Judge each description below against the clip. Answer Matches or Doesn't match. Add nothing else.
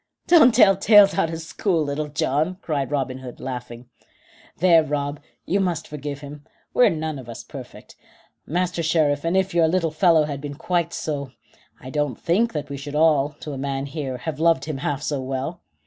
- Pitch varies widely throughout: Doesn't match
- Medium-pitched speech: Matches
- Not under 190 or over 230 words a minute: Matches